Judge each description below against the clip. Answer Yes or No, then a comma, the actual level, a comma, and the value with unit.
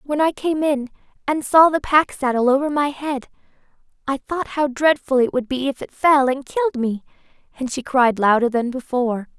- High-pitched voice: Yes, very high, 270 Hz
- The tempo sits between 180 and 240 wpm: Yes, average, 200 wpm